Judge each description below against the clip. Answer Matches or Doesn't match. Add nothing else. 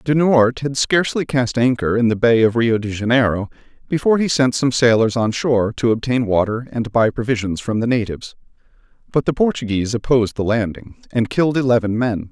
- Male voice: Matches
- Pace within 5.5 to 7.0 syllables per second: Matches